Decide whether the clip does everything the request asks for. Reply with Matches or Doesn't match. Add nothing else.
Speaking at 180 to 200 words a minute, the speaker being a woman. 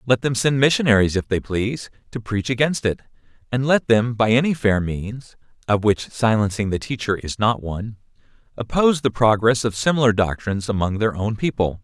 Doesn't match